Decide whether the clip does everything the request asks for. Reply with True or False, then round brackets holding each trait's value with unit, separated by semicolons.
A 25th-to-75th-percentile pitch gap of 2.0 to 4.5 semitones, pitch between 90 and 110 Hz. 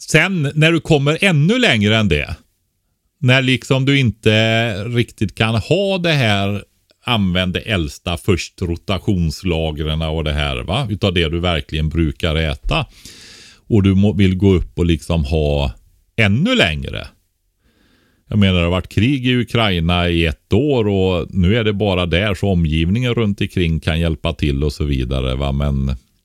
False (5.2 semitones; 95 Hz)